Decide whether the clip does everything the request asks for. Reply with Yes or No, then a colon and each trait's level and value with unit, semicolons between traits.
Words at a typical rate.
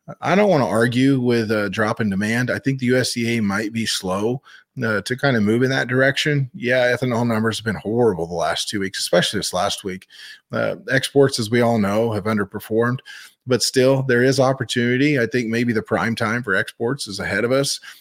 No: fast, 215 wpm